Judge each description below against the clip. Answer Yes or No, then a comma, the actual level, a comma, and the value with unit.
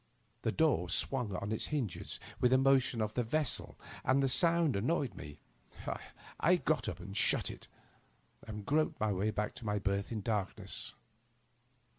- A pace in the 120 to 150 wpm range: No, average, 170 wpm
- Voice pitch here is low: Yes, low, 115 Hz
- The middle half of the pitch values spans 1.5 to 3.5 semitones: No, average, 4.8 semitones